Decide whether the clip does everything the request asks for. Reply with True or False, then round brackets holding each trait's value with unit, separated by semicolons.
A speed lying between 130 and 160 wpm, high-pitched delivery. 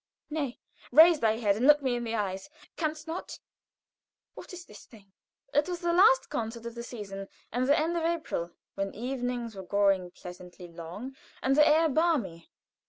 False (180 wpm; 240 Hz)